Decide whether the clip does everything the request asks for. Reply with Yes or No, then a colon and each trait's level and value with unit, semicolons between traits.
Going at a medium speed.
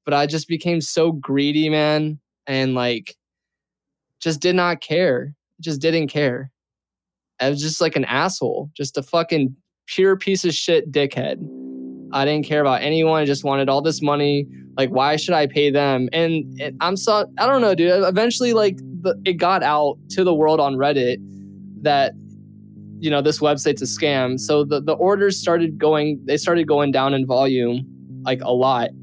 Yes: average, 180 wpm